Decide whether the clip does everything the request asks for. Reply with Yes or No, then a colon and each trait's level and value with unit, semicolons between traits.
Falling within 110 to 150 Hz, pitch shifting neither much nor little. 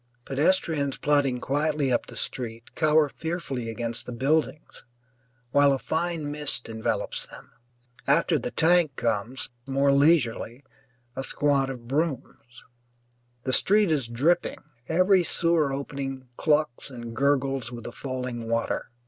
Yes: medium, 140 Hz; average, 3.9 semitones